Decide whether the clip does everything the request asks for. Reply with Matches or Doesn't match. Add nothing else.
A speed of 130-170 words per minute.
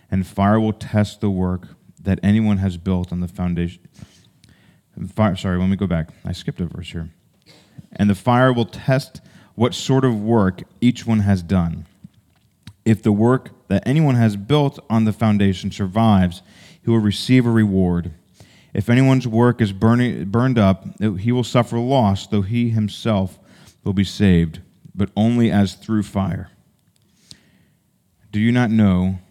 Matches